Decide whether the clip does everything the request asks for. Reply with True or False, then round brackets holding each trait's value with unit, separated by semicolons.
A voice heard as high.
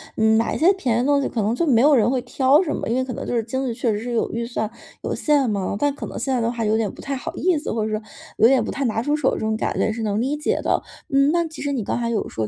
True (245 Hz)